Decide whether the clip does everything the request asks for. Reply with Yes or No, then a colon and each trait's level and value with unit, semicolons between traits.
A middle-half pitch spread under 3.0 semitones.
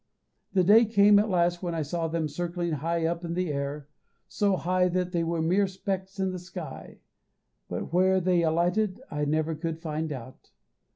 Yes: narrow, 2.5 semitones